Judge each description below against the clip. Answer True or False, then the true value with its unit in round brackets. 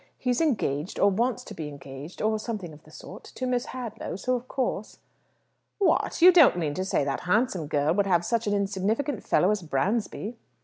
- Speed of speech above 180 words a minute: True (205 wpm)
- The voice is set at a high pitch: True (205 Hz)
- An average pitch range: False (6.7 semitones)